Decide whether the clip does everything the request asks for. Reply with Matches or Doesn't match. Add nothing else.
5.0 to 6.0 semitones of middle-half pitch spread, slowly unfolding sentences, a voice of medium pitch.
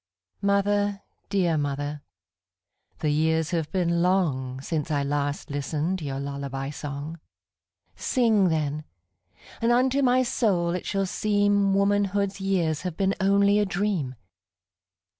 Matches